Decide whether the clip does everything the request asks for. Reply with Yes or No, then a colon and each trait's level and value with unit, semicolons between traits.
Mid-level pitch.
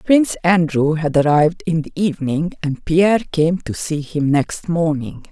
Yes: medium, 165 Hz